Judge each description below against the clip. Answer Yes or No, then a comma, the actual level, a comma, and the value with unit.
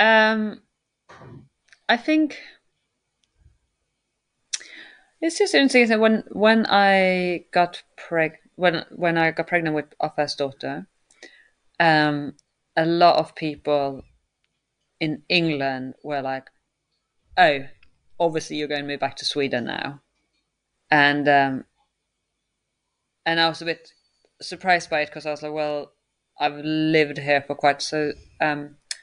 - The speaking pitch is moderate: Yes, medium, 155 Hz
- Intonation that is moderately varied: Yes, average, 3.3 semitones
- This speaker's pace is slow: Yes, slow, 125 wpm